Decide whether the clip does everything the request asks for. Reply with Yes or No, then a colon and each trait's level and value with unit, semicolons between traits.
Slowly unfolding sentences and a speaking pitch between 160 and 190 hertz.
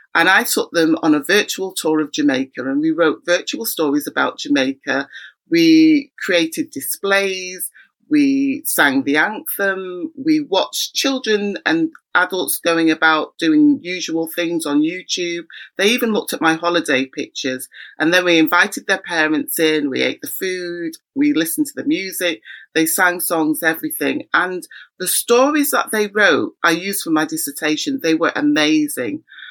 No: average, 155 wpm; medium, 185 Hz